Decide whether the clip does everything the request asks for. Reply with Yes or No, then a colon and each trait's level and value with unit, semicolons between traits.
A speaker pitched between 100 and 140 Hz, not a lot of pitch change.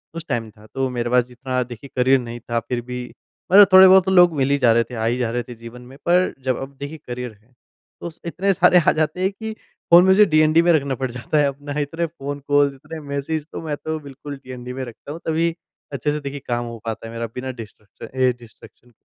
No: low, 135 Hz; average, 4.3 semitones